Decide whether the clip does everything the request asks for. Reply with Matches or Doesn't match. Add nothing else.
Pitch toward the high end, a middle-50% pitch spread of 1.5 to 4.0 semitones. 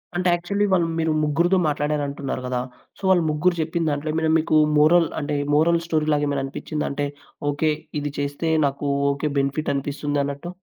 Doesn't match